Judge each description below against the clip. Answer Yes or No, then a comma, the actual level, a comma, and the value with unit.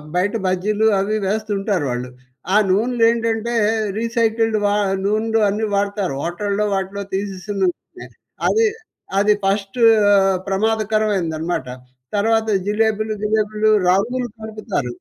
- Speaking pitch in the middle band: No, high, 210 Hz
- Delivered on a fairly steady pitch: Yes, narrow, 2.2 semitones